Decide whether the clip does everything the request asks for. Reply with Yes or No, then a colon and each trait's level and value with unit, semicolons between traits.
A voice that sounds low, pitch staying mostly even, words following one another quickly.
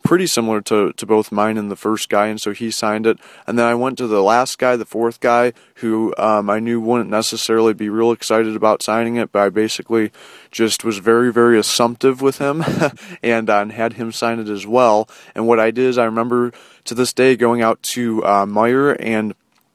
Yes: low, 115 Hz; narrow, 1.9 semitones; fast, 220 wpm